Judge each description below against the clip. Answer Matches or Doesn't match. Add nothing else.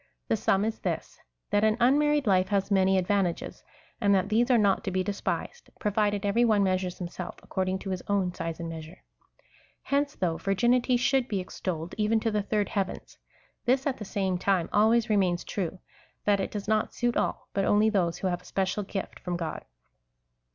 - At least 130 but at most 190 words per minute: Doesn't match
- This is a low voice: Doesn't match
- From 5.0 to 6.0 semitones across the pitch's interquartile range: Doesn't match